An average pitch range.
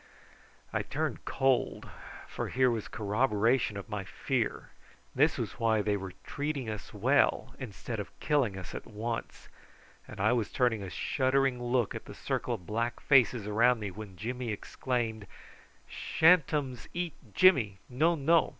Yes: average, 4.1 semitones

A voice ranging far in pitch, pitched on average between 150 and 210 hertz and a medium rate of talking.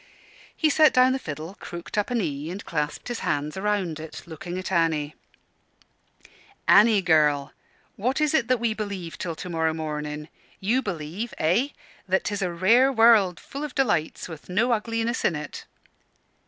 Yes: wide, 6.4 semitones; medium, 185 Hz; average, 170 wpm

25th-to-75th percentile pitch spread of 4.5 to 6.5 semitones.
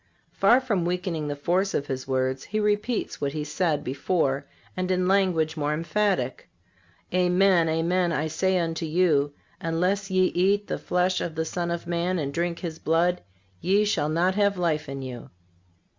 No: average, 3.3 semitones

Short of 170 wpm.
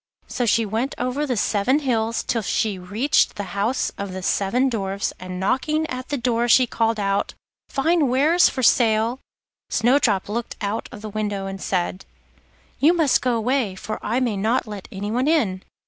No: average, 180 wpm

